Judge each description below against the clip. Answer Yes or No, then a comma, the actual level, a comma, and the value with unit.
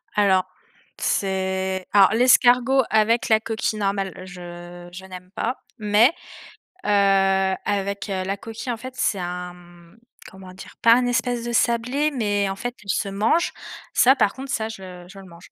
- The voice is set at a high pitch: Yes, high, 200 Hz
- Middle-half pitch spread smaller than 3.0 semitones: No, average, 3.5 semitones